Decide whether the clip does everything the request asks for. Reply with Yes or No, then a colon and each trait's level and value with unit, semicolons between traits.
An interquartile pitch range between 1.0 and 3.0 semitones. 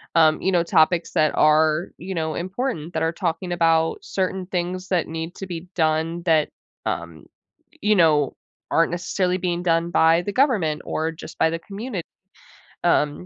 Yes: narrow, 2.4 semitones